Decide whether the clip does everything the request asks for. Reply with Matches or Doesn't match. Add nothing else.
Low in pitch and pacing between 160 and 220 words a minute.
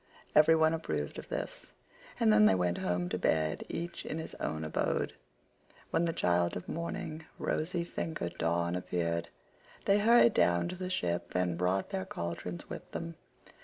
Matches